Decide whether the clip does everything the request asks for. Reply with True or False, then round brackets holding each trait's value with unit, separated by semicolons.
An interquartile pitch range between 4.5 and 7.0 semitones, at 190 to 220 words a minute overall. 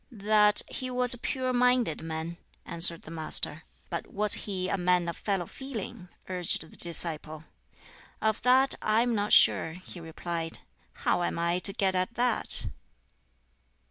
False (5.3 semitones; 155 wpm)